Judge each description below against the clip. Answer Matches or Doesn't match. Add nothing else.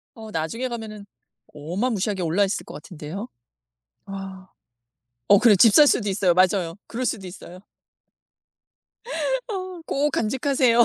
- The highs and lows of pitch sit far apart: Doesn't match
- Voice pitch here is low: Doesn't match